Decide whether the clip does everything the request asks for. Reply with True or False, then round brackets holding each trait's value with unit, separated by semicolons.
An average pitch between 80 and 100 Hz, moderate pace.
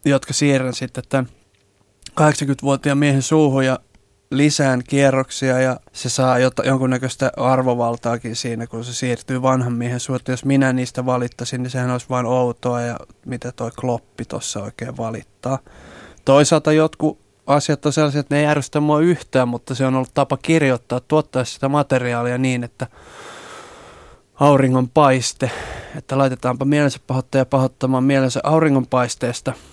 False (130 Hz; 140 wpm)